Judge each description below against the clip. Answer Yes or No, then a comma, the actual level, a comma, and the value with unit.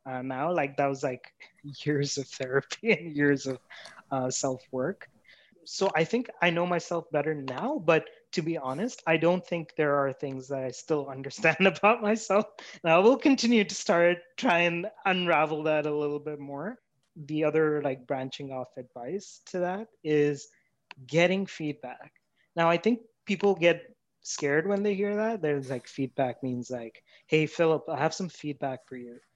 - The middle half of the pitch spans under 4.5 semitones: No, average, 5.0 semitones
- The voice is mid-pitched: Yes, medium, 155 Hz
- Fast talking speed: No, average, 180 wpm